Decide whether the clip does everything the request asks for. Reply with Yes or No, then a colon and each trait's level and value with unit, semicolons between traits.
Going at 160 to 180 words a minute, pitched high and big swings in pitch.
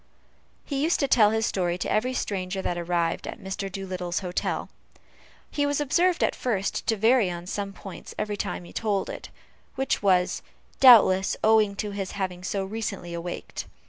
No: average, 175 wpm; high, 200 Hz; average, 3.4 semitones